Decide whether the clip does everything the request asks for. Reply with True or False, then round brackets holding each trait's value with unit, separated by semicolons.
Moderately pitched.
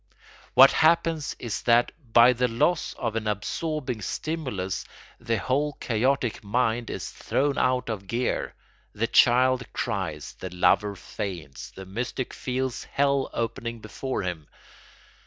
False (120 Hz)